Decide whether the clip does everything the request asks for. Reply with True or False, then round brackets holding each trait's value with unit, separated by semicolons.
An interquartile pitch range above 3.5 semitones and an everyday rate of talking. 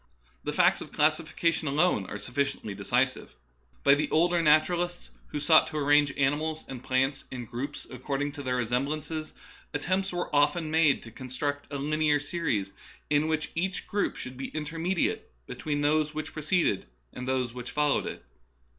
False (3.1 semitones; 165 wpm)